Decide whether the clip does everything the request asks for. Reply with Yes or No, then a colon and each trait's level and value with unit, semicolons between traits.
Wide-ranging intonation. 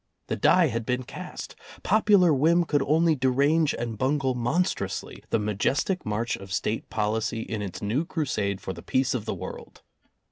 Yes: wide, 6.5 semitones